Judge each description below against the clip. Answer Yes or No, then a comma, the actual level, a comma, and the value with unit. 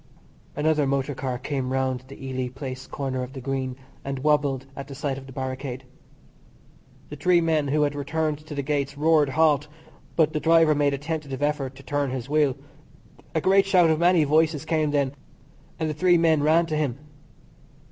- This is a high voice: No, medium, 145 Hz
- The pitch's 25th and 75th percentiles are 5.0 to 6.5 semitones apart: No, average, 2.7 semitones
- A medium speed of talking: Yes, average, 190 wpm